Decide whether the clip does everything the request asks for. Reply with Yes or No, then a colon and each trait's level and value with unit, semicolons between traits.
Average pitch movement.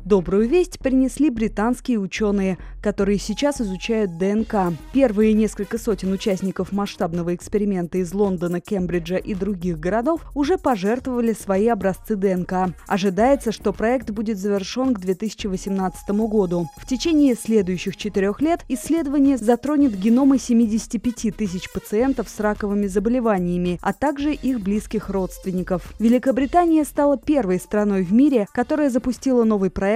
Yes: average, 4.6 semitones